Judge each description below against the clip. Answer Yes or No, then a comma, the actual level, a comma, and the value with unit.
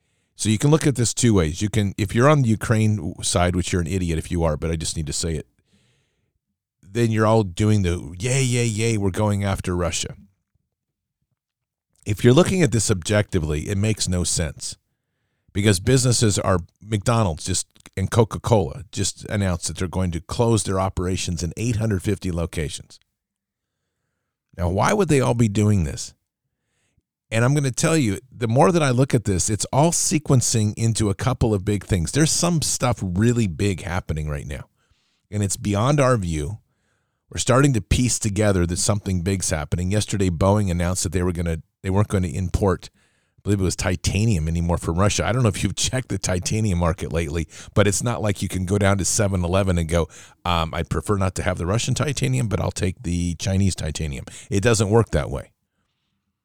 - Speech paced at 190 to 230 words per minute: Yes, average, 200 wpm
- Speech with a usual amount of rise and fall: Yes, average, 4.3 semitones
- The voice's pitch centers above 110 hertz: No, low, 100 Hz